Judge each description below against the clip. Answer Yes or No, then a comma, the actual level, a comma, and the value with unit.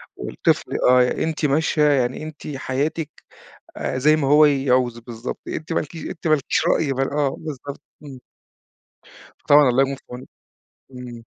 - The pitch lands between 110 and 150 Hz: Yes, medium, 140 Hz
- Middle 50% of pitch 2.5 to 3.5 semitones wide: Yes, average, 3.0 semitones